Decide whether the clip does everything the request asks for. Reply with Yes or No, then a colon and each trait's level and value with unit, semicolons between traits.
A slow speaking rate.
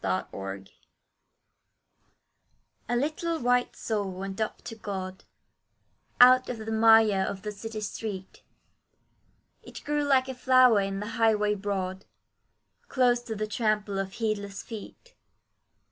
Yes: slow, 130 wpm